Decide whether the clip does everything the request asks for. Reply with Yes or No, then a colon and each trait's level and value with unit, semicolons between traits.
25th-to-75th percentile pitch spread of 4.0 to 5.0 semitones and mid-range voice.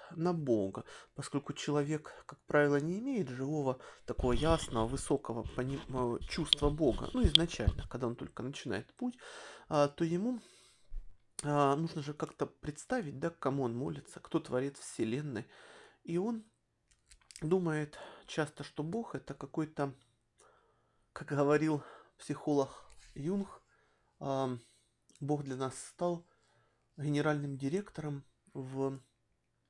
No: average, 3.6 semitones; medium, 145 Hz